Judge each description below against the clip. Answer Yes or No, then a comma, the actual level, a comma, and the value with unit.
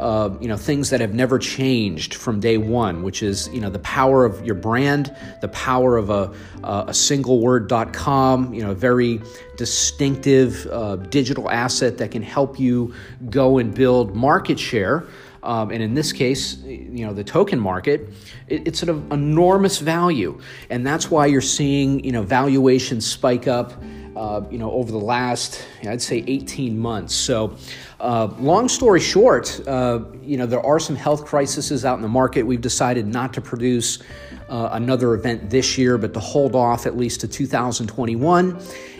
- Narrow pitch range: No, average, 3.1 semitones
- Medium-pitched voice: No, low, 125 Hz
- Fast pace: No, average, 185 wpm